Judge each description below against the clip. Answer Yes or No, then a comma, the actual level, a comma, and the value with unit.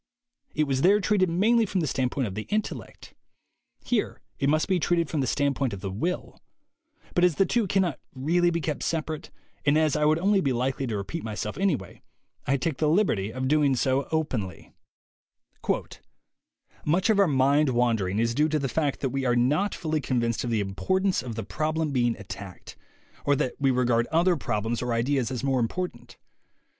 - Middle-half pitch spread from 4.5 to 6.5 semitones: Yes, wide, 5.6 semitones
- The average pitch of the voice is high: No, medium, 140 Hz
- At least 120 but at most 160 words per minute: No, average, 195 wpm